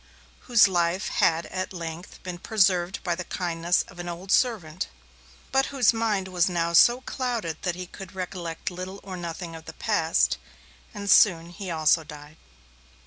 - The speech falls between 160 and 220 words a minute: Yes, average, 165 wpm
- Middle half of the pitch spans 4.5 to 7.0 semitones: No, average, 2.8 semitones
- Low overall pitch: No, medium, 180 Hz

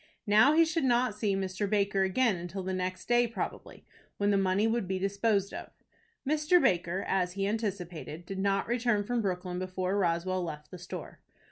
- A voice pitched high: Yes, high, 195 Hz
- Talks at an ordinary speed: Yes, average, 180 wpm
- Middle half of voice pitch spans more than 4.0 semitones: No, average, 3.4 semitones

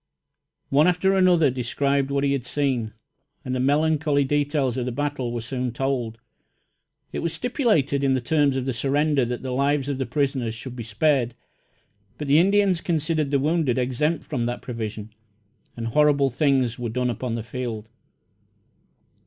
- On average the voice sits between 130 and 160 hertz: Yes, low, 135 Hz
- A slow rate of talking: No, average, 170 wpm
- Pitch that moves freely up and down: No, average, 3.2 semitones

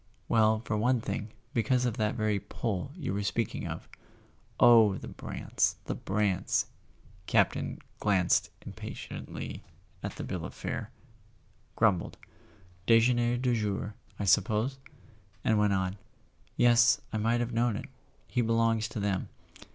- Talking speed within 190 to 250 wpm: No, slow, 135 wpm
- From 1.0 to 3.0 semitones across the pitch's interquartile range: Yes, narrow, 2.6 semitones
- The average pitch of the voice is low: Yes, low, 110 Hz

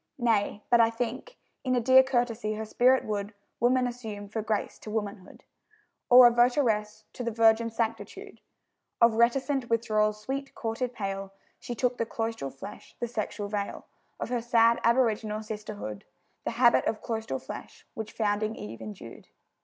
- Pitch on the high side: Yes, high, 225 Hz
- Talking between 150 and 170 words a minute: Yes, average, 155 wpm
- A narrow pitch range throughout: Yes, narrow, 2.3 semitones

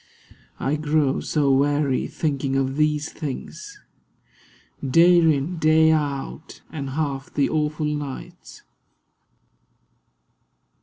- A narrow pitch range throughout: Yes, narrow, 2.2 semitones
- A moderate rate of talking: No, slow, 95 wpm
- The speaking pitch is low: No, medium, 150 Hz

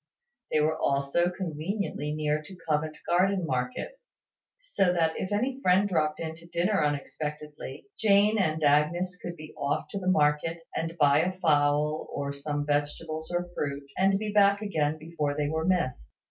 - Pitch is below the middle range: No, medium, 160 Hz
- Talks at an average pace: Yes, average, 165 wpm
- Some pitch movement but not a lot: Yes, average, 3.8 semitones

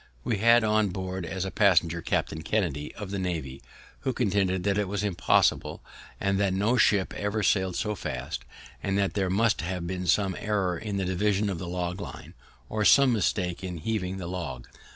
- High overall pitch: No, very low, 95 Hz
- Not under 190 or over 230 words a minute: Yes, average, 195 wpm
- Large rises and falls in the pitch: No, narrow, 2.5 semitones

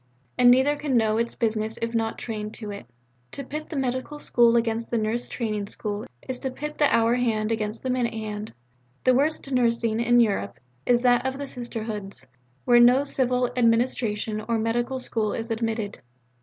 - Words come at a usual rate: Yes, average, 180 wpm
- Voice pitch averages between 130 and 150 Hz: No, high, 235 Hz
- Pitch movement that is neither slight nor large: No, narrow, 2.3 semitones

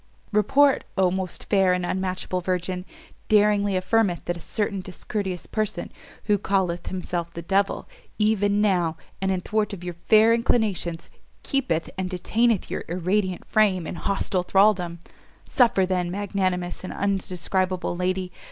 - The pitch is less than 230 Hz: Yes, high, 190 Hz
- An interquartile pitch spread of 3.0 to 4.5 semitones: No, narrow, 2.5 semitones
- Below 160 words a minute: Yes, average, 140 wpm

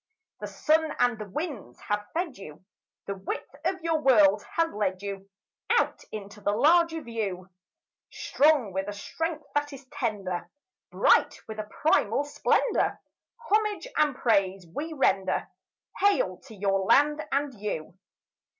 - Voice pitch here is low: No, high, 230 Hz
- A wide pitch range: Yes, wide, 7.6 semitones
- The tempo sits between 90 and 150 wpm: Yes, average, 140 wpm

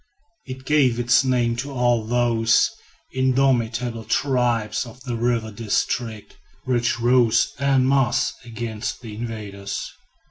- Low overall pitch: Yes, low, 120 Hz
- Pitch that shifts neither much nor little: No, narrow, 2.1 semitones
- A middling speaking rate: No, slow, 115 wpm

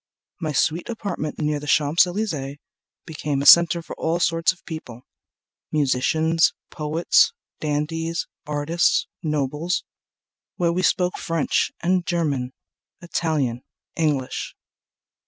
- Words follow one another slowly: Yes, slow, 110 wpm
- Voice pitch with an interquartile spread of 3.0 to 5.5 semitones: No, narrow, 2.6 semitones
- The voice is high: No, medium, 160 Hz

